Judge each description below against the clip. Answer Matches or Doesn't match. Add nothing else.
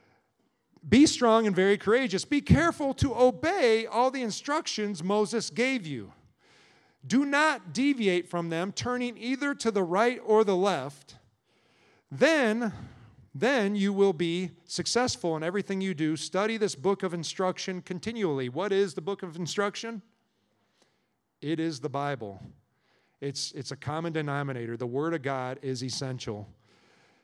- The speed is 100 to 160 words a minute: Matches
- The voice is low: Doesn't match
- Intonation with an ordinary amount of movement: Doesn't match